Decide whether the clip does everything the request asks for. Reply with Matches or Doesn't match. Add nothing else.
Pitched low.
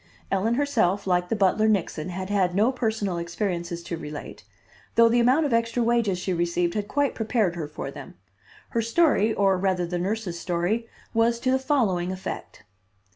Doesn't match